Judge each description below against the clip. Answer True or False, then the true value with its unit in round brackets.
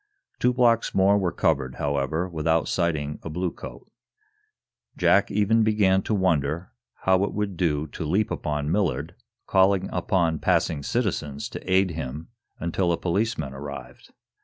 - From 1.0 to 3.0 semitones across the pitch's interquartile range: False (4.3 semitones)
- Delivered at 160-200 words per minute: False (140 wpm)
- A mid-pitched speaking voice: False (85 Hz)